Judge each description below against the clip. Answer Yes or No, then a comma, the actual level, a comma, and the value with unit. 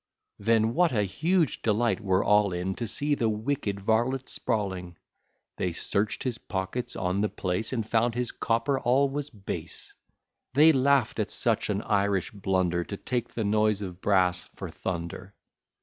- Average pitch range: Yes, average, 4.2 semitones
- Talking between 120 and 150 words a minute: No, average, 165 wpm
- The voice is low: Yes, low, 105 Hz